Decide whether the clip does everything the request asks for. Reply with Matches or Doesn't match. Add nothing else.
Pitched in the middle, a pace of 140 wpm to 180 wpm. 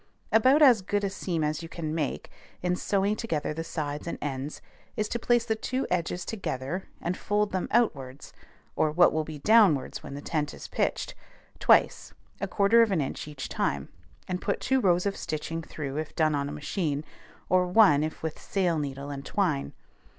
Doesn't match